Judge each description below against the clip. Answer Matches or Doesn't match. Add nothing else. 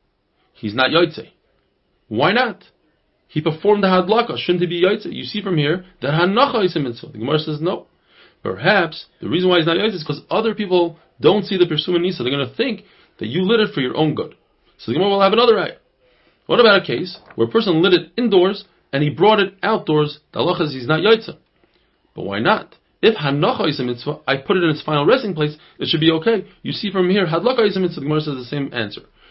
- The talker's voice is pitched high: Doesn't match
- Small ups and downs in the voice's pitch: Doesn't match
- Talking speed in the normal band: Doesn't match